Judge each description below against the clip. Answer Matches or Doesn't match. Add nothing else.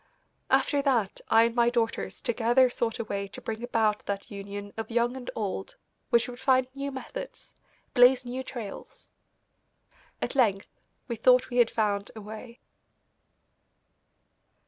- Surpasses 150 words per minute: Doesn't match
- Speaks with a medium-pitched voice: Doesn't match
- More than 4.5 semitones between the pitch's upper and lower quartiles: Doesn't match